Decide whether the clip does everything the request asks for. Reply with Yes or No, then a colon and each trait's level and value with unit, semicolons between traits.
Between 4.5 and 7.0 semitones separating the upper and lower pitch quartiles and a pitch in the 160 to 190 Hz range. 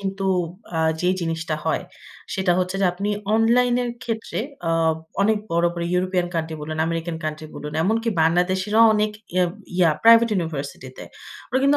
Yes: average, 4.9 semitones; medium, 185 Hz